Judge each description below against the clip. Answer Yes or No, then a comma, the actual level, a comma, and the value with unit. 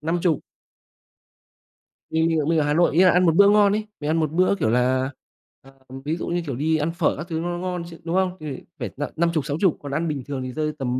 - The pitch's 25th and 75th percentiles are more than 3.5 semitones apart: No, average, 3.2 semitones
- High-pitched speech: No, medium, 160 Hz